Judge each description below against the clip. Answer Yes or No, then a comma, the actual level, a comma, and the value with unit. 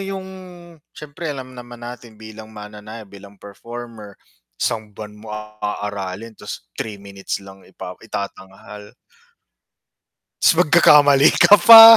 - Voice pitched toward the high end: No, low, 110 Hz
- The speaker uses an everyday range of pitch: Yes, average, 3.4 semitones